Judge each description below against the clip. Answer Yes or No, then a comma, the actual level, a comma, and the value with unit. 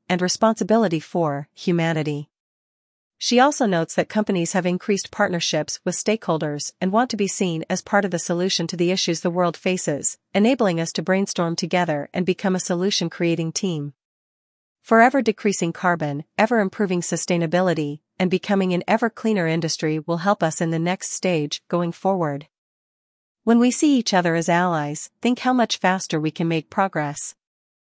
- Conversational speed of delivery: Yes, average, 165 wpm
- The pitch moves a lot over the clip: No, average, 3.5 semitones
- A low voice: No, medium, 180 Hz